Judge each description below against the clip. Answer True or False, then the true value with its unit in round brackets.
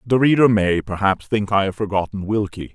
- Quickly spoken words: False (195 wpm)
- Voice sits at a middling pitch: False (105 Hz)